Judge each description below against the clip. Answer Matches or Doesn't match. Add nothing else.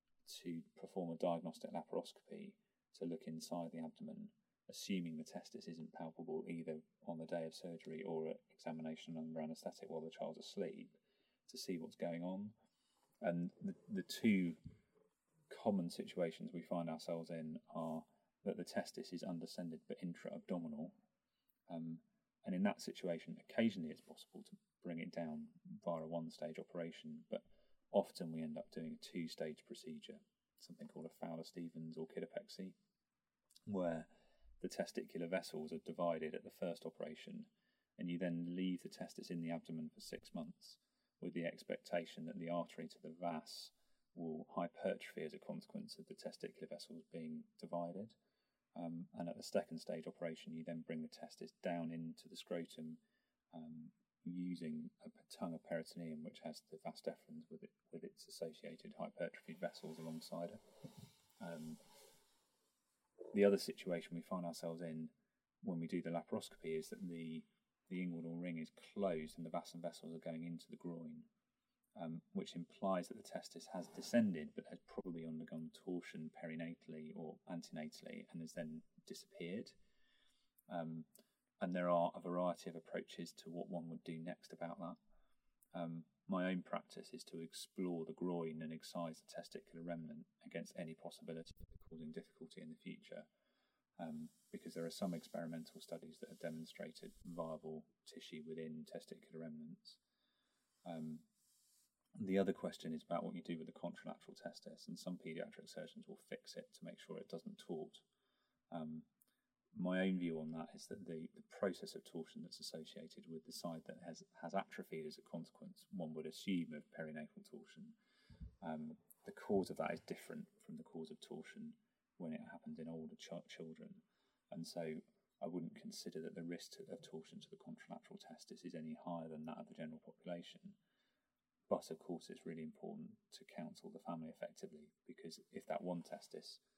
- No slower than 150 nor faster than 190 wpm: Matches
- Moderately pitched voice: Doesn't match